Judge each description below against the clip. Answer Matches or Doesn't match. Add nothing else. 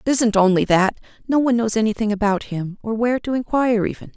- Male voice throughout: Doesn't match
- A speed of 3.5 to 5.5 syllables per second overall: Doesn't match